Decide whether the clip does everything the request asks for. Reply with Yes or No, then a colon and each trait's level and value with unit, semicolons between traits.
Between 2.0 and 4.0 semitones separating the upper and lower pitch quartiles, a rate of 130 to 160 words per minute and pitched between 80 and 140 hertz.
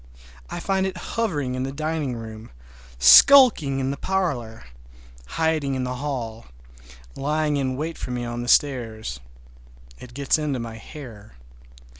No: average, 4.5 semitones; average, 145 wpm; low, 135 Hz